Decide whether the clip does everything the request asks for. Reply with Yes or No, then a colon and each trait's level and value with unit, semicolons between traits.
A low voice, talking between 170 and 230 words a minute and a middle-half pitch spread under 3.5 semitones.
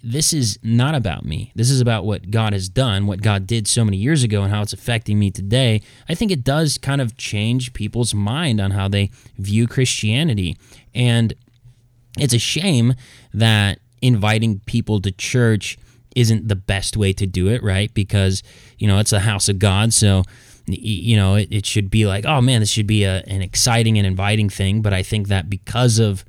Yes: low, 110 Hz; average, 200 wpm; average, 3.1 semitones